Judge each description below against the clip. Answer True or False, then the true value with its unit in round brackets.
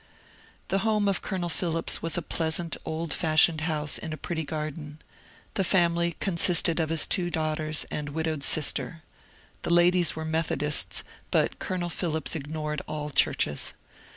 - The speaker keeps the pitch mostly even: True (2.0 semitones)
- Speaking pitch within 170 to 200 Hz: False (160 Hz)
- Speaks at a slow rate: False (150 wpm)